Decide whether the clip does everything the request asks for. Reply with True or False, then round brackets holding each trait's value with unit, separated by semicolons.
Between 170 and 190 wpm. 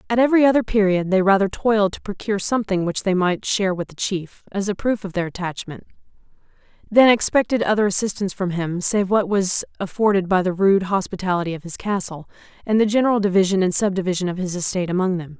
False (200 wpm)